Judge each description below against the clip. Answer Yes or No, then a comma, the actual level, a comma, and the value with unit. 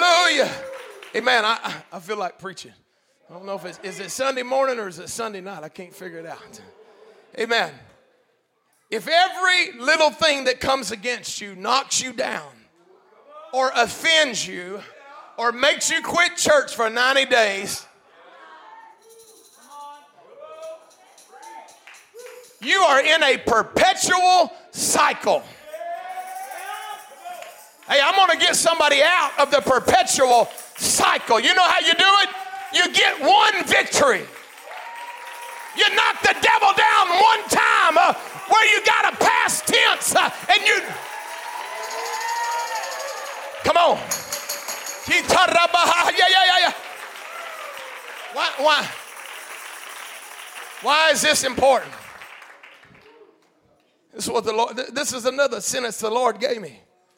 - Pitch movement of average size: No, wide, 7.7 semitones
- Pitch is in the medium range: No, very high, 325 Hz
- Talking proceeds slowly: Yes, slow, 120 wpm